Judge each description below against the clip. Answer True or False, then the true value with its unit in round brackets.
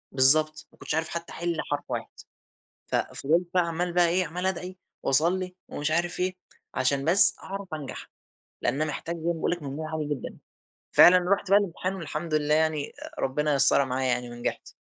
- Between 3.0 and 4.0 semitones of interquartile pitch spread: True (3.4 semitones)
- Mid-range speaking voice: True (160 Hz)